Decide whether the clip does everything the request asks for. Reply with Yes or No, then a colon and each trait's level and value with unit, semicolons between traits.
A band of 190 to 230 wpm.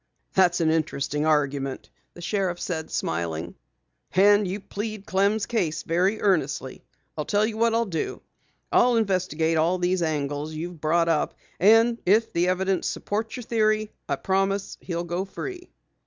No: average, 155 wpm